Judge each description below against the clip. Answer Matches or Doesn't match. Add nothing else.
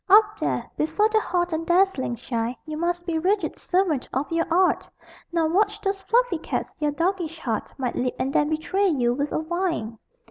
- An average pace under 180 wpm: Doesn't match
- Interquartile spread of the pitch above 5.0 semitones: Doesn't match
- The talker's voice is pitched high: Matches